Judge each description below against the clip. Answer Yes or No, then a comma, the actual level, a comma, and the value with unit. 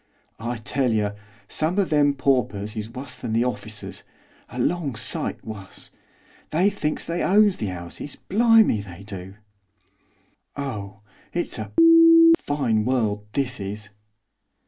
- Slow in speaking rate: Yes, slow, 130 wpm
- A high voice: No, low, 120 Hz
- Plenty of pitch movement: Yes, wide, 5.9 semitones